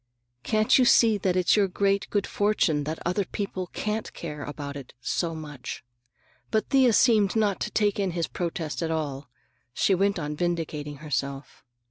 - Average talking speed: Yes, average, 170 wpm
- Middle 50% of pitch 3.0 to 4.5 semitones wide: No, wide, 5.4 semitones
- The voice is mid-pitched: Yes, medium, 175 Hz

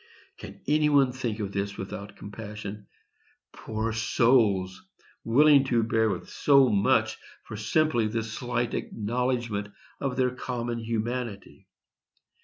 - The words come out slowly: Yes, slow, 120 wpm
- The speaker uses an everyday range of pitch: Yes, average, 3.3 semitones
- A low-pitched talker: Yes, low, 115 Hz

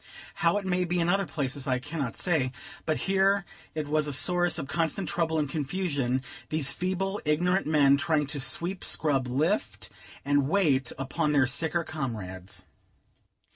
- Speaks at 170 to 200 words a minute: No, average, 160 wpm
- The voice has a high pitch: No, medium, 155 Hz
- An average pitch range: Yes, average, 4.6 semitones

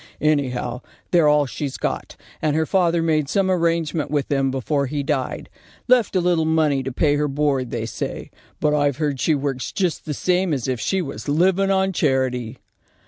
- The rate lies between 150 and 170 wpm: No, average, 195 wpm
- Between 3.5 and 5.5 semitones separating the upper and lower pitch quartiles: Yes, average, 3.8 semitones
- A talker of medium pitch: Yes, medium, 150 Hz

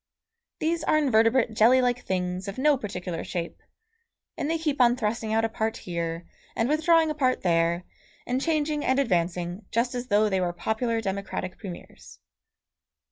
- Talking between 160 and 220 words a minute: Yes, average, 165 wpm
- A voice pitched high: Yes, high, 225 Hz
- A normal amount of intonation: No, wide, 6.1 semitones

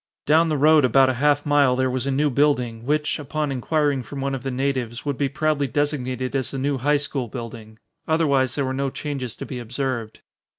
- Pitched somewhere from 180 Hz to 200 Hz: No, low, 135 Hz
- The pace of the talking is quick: Yes, fast, 215 wpm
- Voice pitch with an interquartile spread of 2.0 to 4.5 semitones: Yes, narrow, 2.4 semitones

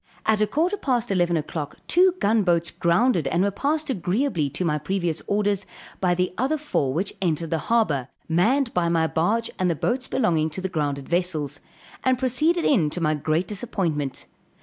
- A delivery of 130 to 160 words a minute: No, average, 185 wpm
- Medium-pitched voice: Yes, medium, 180 Hz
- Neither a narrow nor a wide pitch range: No, wide, 6.6 semitones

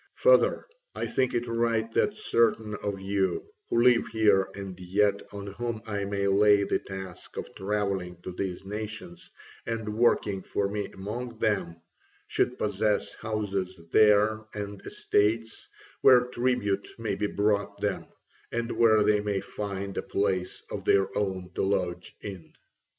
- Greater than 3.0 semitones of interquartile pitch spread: No, narrow, 2.4 semitones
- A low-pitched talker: Yes, low, 105 Hz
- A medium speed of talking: Yes, average, 150 wpm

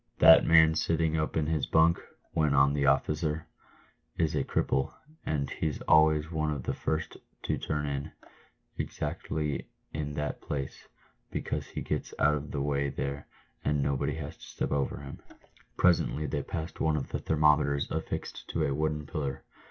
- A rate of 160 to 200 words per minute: Yes, average, 165 wpm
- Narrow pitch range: Yes, narrow, 1.8 semitones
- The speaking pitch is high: No, very low, 75 Hz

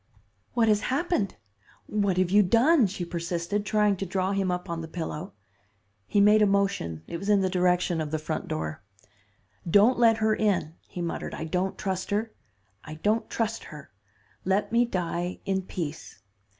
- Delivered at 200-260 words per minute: No, average, 175 wpm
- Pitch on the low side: No, high, 190 Hz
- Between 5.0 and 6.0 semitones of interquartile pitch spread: No, average, 3.5 semitones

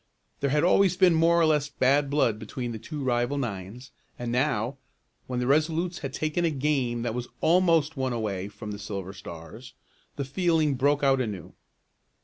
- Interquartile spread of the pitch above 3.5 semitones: Yes, average, 4.7 semitones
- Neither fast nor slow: Yes, average, 180 wpm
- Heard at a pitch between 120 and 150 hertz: Yes, low, 135 Hz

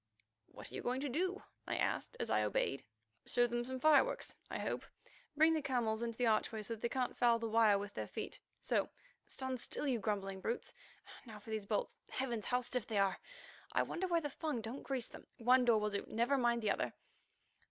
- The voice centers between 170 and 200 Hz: No, high, 240 Hz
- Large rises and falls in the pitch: No, average, 3.6 semitones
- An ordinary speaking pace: No, fast, 210 wpm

